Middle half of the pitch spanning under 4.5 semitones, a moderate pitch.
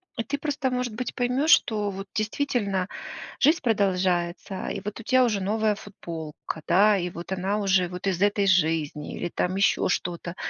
No: average, 3.8 semitones; high, 200 Hz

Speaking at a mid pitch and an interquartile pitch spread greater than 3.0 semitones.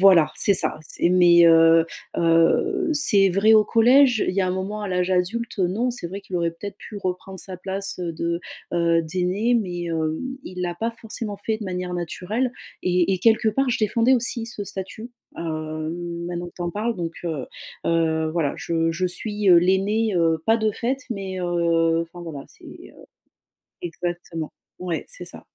Yes: medium, 180 Hz; average, 3.9 semitones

